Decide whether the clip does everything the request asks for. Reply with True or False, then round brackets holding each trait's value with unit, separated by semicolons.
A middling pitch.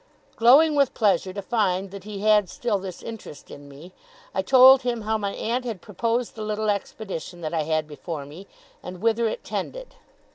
False (210 Hz)